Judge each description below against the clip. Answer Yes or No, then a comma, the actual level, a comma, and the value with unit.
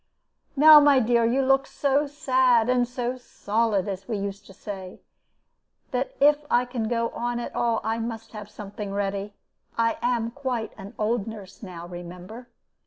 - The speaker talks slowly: No, average, 170 wpm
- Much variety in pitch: No, average, 3.6 semitones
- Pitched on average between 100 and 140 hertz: No, high, 230 Hz